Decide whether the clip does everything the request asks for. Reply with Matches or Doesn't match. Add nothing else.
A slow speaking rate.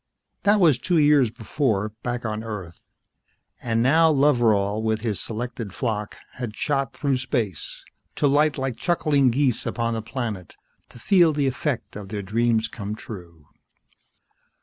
Doesn't match